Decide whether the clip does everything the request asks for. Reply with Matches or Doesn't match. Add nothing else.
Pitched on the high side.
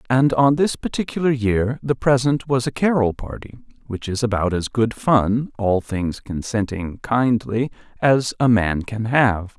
Doesn't match